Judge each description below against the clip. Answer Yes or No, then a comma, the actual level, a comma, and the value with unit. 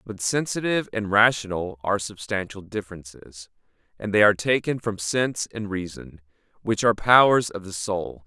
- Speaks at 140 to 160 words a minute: Yes, average, 150 wpm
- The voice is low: Yes, low, 100 Hz